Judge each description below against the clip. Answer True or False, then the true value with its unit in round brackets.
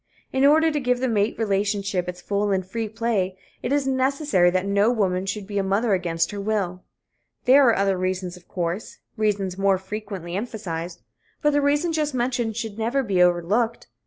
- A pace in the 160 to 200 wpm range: True (190 wpm)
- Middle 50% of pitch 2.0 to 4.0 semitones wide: False (4.5 semitones)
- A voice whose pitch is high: True (205 Hz)